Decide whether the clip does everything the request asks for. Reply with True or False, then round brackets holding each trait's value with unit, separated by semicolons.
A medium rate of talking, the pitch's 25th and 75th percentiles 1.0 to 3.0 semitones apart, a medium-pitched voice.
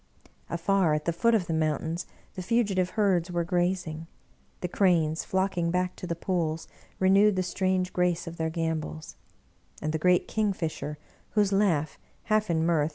True (170 wpm; 2.7 semitones; 175 Hz)